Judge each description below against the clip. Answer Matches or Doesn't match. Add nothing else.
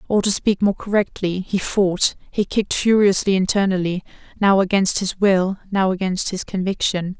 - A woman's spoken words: Matches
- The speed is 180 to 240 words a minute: Doesn't match